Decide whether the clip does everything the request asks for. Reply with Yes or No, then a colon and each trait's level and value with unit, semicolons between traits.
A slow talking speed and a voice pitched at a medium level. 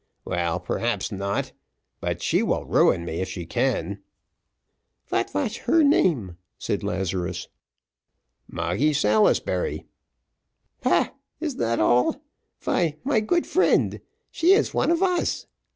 No: slow, 120 wpm; low, 120 Hz